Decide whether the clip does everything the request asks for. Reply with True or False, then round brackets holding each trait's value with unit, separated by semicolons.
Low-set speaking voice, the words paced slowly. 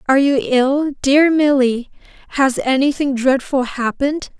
False (270 Hz; 125 wpm)